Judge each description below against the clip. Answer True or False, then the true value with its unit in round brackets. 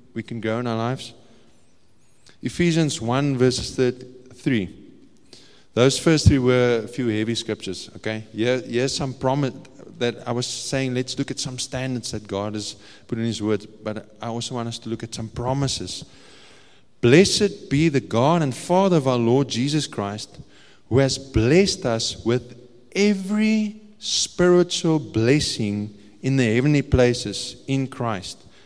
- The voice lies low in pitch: True (125 Hz)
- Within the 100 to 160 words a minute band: True (155 wpm)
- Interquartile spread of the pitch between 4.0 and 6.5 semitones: False (3.4 semitones)